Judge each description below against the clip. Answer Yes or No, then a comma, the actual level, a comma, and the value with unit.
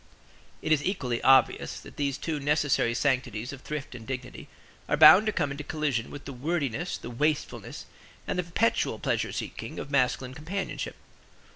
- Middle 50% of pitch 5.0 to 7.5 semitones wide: No, average, 3.4 semitones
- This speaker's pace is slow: No, average, 165 wpm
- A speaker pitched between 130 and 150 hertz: Yes, medium, 140 Hz